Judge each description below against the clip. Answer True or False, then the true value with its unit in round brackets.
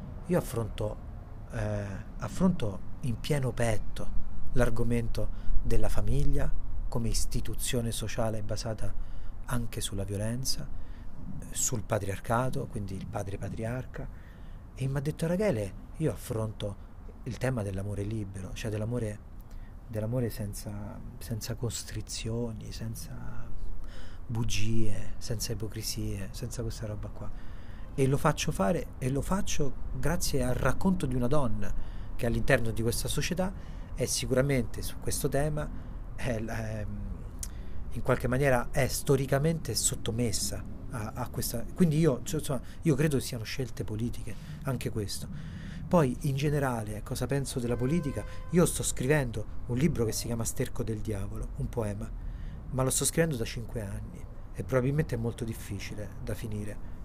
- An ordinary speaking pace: True (135 wpm)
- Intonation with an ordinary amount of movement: True (3.7 semitones)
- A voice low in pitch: True (115 Hz)